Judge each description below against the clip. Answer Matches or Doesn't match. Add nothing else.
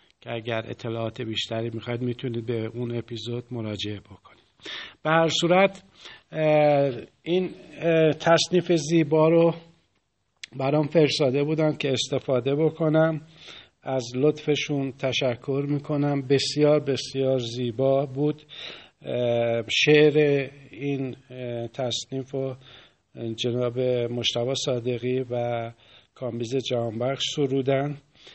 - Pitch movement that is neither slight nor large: Matches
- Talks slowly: Matches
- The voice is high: Doesn't match